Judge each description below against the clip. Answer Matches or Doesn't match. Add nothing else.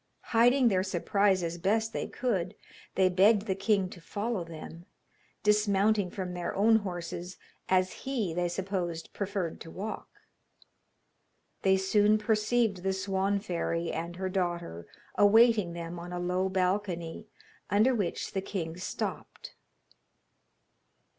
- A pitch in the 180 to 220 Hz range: Matches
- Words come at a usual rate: Doesn't match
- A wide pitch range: Doesn't match